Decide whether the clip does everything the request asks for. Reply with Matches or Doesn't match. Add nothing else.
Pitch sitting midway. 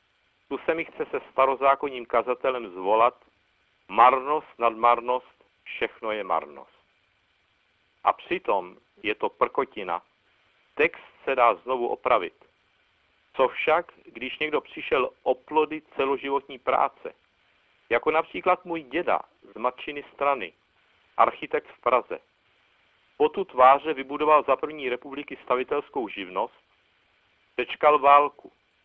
Matches